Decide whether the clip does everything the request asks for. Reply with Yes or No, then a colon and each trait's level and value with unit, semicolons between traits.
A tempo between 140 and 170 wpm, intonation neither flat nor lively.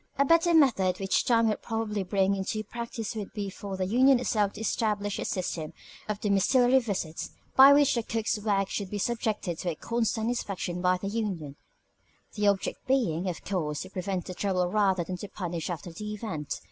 No: average, 190 wpm; average, 3.5 semitones